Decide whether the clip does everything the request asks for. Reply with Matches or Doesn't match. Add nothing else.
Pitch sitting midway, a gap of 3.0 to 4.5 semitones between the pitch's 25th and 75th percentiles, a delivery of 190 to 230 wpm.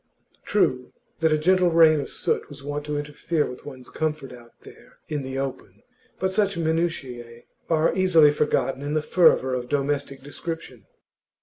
Doesn't match